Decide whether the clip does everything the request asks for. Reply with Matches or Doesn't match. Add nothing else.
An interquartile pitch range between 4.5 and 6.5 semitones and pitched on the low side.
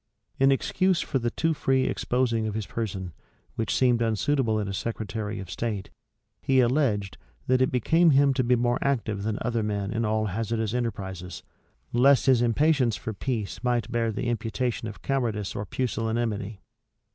Doesn't match